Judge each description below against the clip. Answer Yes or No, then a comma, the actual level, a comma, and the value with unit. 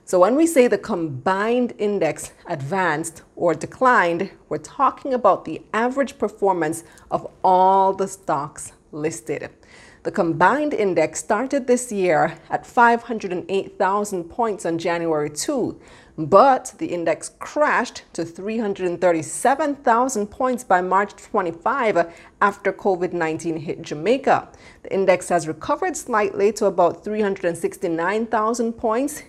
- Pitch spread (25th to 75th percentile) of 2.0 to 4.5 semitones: No, average, 5.3 semitones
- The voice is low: No, high, 195 Hz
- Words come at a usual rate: No, slow, 115 wpm